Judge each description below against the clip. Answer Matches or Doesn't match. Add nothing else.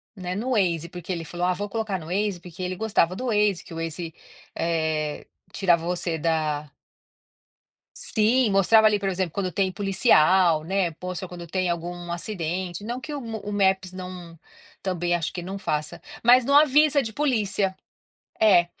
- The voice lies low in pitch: Doesn't match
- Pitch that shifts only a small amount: Doesn't match